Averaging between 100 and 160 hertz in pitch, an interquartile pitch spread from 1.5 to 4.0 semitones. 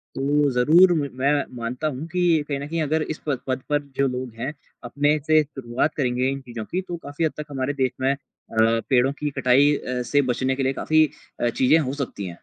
Yes: medium, 140 Hz; average, 2.9 semitones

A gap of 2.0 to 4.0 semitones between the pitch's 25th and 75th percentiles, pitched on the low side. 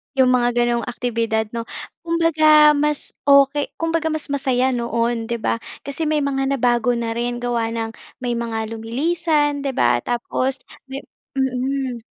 No: average, 3.5 semitones; very high, 255 Hz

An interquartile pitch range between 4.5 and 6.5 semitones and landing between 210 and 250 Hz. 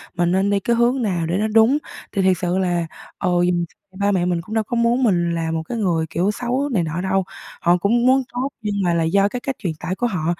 No: average, 5.1 semitones; high, 195 Hz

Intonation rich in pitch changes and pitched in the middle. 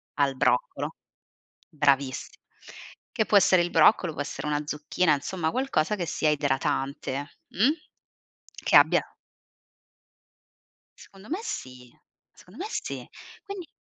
Yes: wide, 6.3 semitones; medium, 155 Hz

